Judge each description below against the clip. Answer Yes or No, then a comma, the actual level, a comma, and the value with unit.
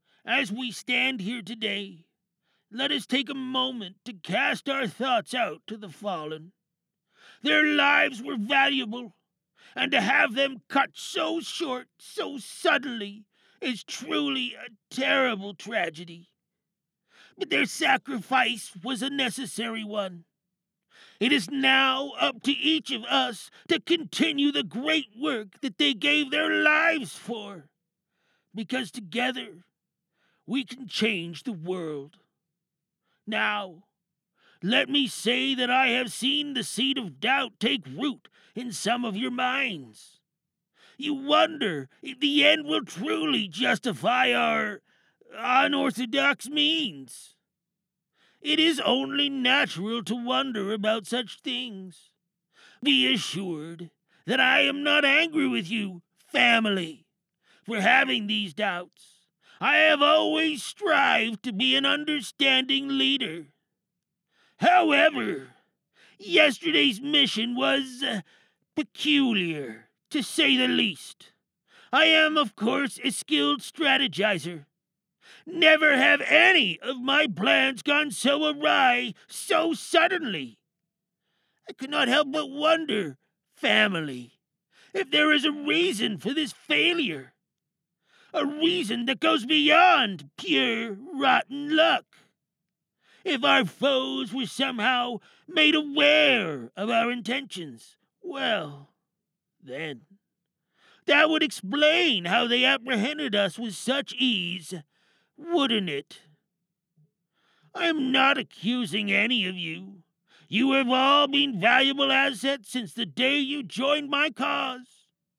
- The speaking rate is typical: No, slow, 120 wpm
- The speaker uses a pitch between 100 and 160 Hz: No, very high, 250 Hz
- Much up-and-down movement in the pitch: Yes, wide, 6.4 semitones